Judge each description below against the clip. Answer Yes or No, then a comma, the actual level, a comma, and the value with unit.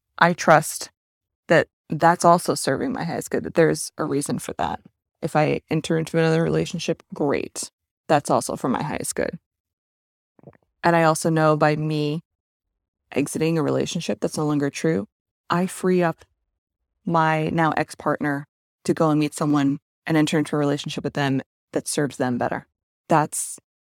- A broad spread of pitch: No, narrow, 2.6 semitones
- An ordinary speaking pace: Yes, average, 165 wpm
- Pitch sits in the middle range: Yes, medium, 155 Hz